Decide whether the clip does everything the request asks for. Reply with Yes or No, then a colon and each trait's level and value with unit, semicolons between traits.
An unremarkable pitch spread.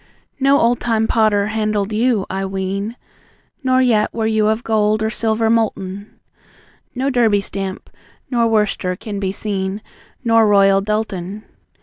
No: narrow, 2.3 semitones